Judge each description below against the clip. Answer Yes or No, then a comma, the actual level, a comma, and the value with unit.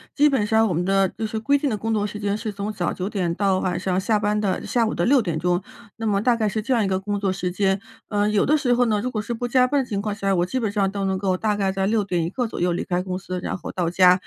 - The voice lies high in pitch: Yes, high, 205 Hz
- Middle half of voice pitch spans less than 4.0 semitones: Yes, average, 2.9 semitones